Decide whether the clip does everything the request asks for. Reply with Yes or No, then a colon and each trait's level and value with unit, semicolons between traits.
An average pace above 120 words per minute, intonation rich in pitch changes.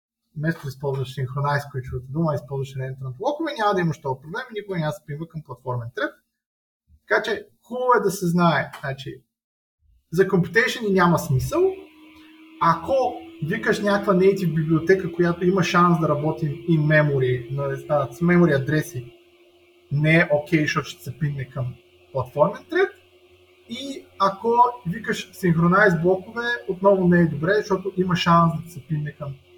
Yes: average, 160 wpm; wide, 6.3 semitones